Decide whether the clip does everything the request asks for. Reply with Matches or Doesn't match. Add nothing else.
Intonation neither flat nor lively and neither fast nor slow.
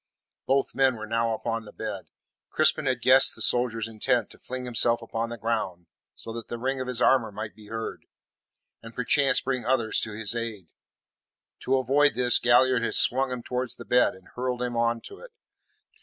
Doesn't match